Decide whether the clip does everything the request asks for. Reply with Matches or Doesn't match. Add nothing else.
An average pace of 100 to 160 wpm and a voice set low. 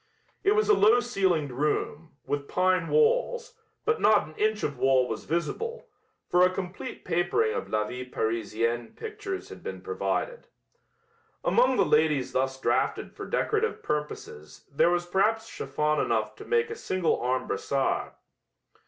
Doesn't match